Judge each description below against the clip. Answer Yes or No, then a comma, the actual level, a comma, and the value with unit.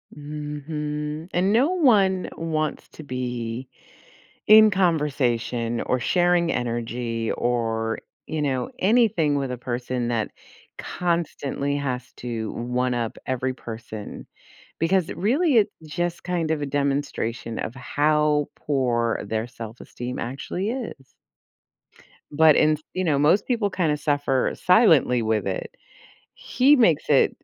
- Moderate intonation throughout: No, wide, 5.9 semitones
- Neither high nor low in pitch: Yes, medium, 145 Hz